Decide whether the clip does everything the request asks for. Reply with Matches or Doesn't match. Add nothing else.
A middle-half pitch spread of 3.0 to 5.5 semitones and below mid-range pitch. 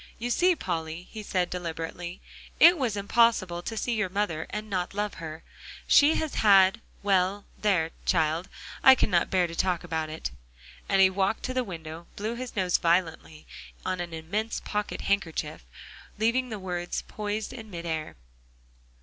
Doesn't match